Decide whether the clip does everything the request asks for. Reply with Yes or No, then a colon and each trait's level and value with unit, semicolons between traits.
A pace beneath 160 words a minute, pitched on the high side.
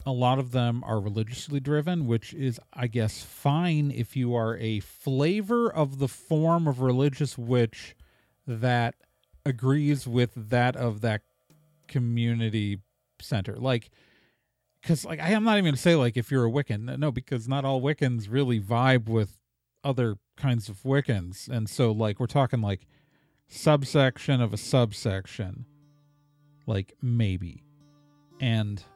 No: average, 145 wpm; low, 125 Hz